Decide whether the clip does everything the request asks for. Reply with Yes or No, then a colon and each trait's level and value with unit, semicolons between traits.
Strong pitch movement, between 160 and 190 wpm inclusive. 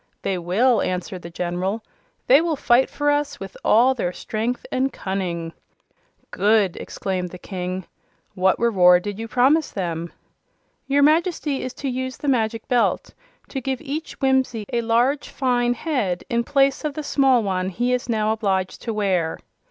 Yes: wide, 5.9 semitones; average, 165 wpm